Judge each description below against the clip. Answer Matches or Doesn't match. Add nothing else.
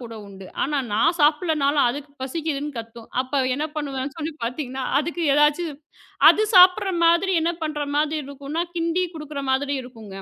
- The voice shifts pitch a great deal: Doesn't match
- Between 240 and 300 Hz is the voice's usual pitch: Matches